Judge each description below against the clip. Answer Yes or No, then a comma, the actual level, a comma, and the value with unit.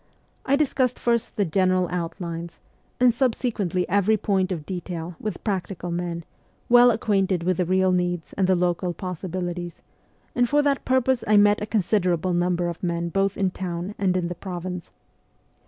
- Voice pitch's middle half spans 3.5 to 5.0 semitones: No, average, 3.1 semitones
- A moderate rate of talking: Yes, average, 165 wpm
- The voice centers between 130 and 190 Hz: Yes, medium, 185 Hz